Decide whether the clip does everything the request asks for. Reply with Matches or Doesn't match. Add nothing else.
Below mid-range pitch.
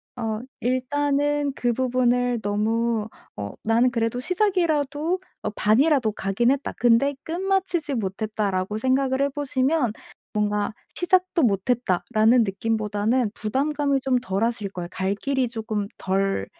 Doesn't match